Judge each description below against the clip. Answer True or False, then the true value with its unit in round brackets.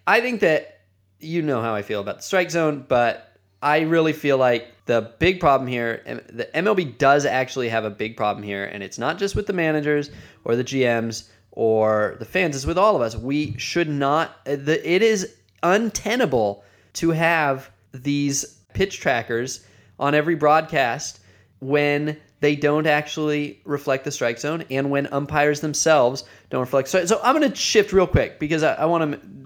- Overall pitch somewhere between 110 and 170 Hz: True (140 Hz)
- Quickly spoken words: False (185 wpm)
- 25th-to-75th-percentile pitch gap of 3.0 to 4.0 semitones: False (5.3 semitones)